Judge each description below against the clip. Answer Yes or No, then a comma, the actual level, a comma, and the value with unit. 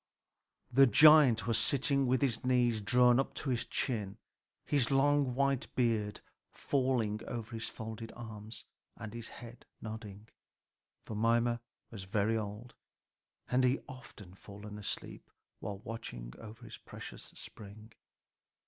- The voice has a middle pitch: No, low, 115 Hz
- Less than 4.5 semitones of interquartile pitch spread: Yes, average, 3.0 semitones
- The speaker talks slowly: Yes, slow, 130 wpm